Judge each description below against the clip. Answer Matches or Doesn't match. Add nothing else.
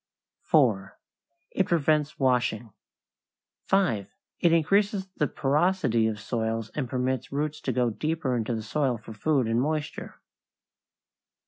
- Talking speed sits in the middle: Doesn't match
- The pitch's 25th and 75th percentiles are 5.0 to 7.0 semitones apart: Matches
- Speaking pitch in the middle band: Doesn't match